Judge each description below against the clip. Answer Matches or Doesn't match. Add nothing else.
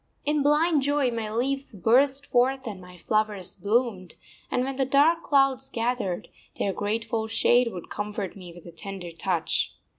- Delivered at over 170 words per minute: Doesn't match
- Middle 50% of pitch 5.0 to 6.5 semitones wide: Matches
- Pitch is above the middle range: Matches